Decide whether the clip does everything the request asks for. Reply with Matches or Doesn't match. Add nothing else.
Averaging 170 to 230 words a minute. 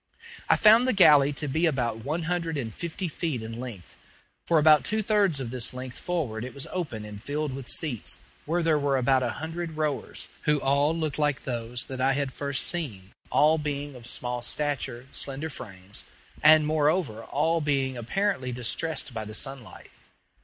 Matches